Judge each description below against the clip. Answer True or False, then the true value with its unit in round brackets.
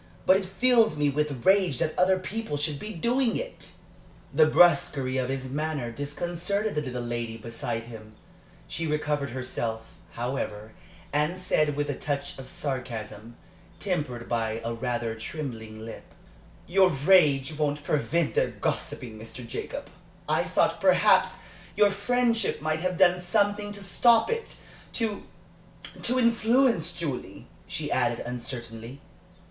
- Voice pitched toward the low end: False (150 Hz)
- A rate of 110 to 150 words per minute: True (140 wpm)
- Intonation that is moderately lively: False (7.5 semitones)